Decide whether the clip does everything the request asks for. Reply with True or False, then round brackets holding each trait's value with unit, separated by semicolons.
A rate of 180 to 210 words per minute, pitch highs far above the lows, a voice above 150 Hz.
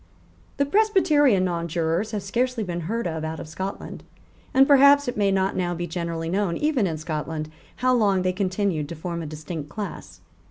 True (185 wpm; 5.9 semitones; 185 Hz)